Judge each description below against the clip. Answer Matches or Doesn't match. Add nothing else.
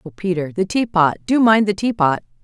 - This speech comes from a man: Doesn't match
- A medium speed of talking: Matches